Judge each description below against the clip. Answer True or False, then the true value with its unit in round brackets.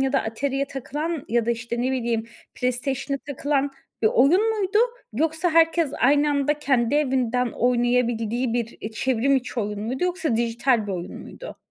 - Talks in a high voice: True (260 Hz)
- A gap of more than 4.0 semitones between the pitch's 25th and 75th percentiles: False (3.5 semitones)